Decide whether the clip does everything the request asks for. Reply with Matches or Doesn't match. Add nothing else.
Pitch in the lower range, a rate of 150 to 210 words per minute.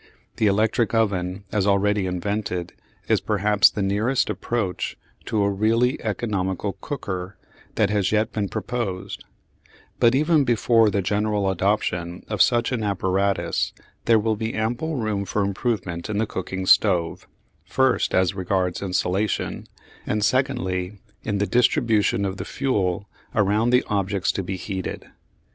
Doesn't match